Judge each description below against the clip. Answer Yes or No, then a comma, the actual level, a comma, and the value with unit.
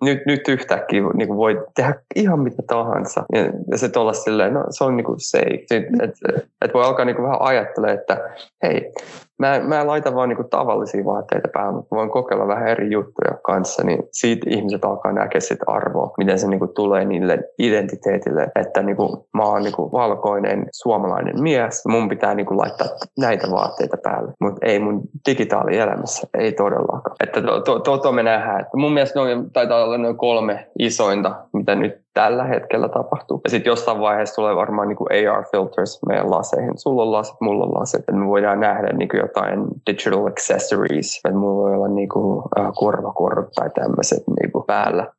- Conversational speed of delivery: No, fast, 180 wpm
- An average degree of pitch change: Yes, average, 5.0 semitones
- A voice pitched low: Yes, low, 115 Hz